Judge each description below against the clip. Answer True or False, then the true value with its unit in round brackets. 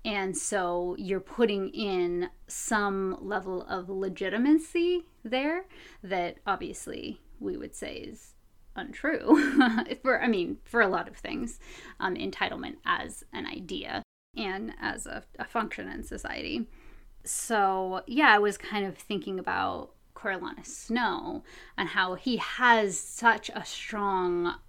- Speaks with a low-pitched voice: False (205 Hz)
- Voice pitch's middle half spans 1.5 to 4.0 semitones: False (5.2 semitones)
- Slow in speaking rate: True (130 wpm)